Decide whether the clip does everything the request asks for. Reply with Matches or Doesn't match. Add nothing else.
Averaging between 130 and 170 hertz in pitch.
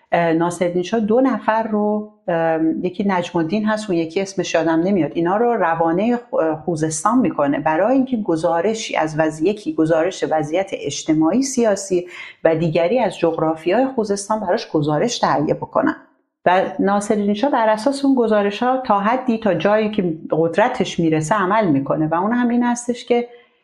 Doesn't match